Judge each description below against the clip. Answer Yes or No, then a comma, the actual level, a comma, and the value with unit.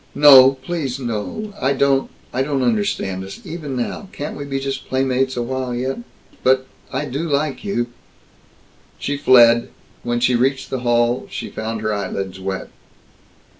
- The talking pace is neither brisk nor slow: Yes, average, 160 wpm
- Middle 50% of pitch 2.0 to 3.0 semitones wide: Yes, average, 2.7 semitones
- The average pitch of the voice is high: No, low, 130 Hz